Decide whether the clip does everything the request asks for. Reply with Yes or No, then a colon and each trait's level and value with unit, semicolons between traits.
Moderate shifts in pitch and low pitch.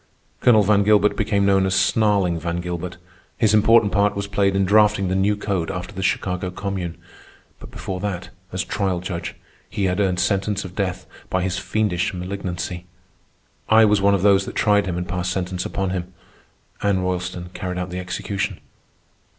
No: narrow, 2.0 semitones; very low, 95 Hz